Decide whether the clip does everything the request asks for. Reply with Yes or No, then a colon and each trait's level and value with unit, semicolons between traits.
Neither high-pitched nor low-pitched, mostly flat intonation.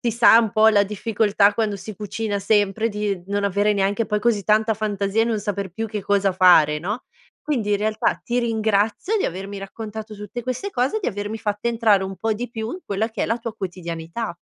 No: high, 210 Hz; narrow, 2.0 semitones